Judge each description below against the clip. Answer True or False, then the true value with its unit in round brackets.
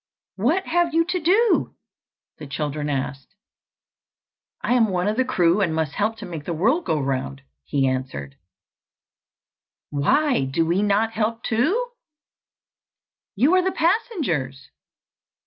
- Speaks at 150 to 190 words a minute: False (135 wpm)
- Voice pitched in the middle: False (205 Hz)